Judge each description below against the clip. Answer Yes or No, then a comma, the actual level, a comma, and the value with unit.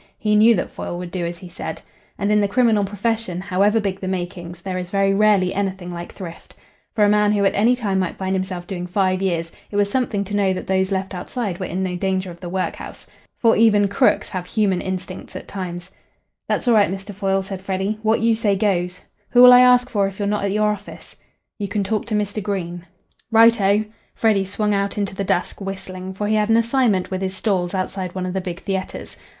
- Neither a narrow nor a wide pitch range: No, narrow, 2.2 semitones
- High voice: Yes, high, 195 Hz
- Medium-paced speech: No, fast, 230 wpm